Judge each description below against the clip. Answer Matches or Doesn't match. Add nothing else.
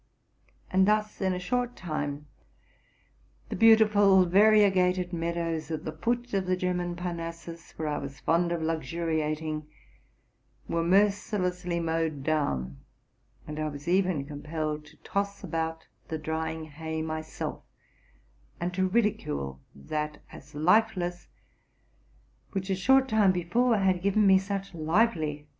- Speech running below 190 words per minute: Matches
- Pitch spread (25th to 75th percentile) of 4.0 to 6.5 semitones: Doesn't match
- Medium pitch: Matches